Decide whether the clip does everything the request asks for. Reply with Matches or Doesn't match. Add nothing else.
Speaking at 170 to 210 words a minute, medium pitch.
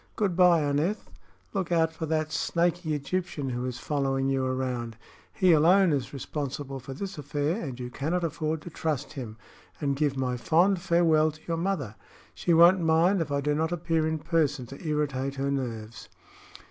Matches